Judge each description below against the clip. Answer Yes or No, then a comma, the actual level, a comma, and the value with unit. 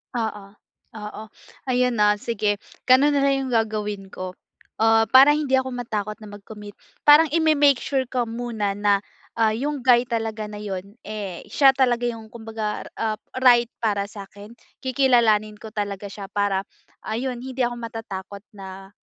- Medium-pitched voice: No, high, 225 Hz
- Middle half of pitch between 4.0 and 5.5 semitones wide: No, average, 3.3 semitones